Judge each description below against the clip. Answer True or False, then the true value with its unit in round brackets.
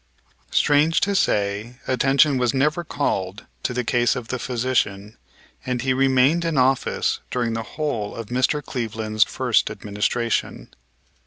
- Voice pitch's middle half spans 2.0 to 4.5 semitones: True (3.2 semitones)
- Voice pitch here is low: True (125 Hz)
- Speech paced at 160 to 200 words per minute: False (140 wpm)